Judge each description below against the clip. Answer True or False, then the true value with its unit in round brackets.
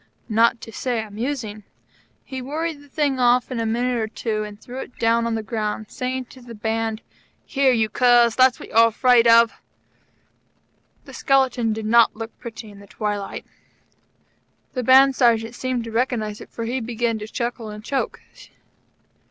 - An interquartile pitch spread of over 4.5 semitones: False (2.4 semitones)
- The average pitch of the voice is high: True (235 Hz)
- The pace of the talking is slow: False (175 wpm)